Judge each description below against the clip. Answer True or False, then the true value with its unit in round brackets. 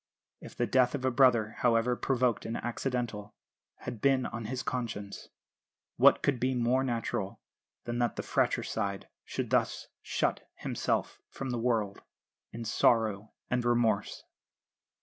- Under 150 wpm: True (140 wpm)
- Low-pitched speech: True (120 Hz)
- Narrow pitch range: True (2.1 semitones)